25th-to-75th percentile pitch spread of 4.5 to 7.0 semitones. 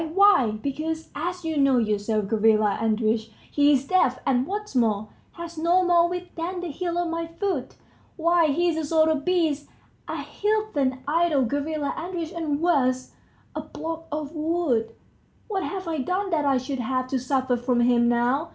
Yes: average, 5.1 semitones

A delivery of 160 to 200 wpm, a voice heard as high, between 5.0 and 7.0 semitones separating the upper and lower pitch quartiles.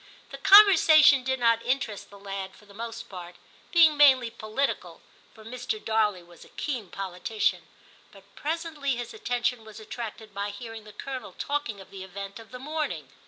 Yes: average, 175 wpm; high, 230 Hz; average, 5.3 semitones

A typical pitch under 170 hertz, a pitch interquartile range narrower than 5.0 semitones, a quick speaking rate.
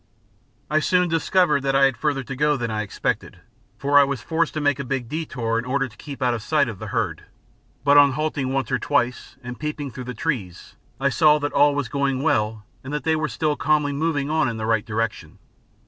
Yes: medium, 140 Hz; average, 3.4 semitones; fast, 230 wpm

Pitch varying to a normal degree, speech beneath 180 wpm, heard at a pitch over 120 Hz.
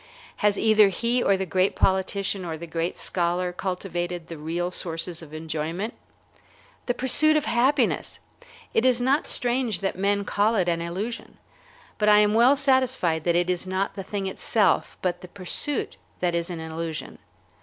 Yes: average, 4.4 semitones; average, 170 wpm; high, 190 Hz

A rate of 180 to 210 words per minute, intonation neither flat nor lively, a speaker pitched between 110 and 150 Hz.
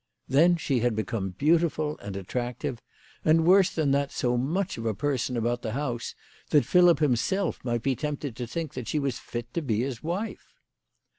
Yes: average, 190 wpm; average, 5.0 semitones; low, 135 Hz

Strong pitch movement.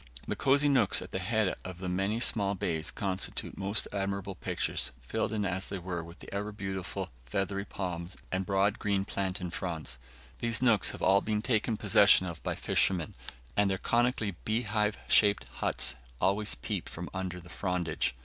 No: narrow, 2.6 semitones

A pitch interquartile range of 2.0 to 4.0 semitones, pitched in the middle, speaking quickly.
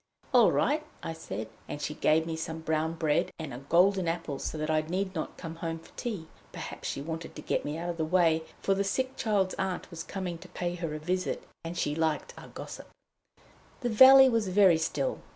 Yes: average, 3.1 semitones; medium, 165 Hz; fast, 220 wpm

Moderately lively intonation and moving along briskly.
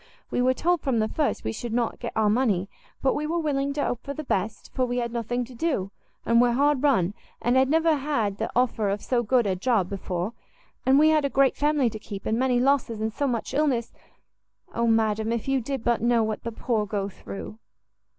Yes: average, 4.0 semitones; fast, 230 wpm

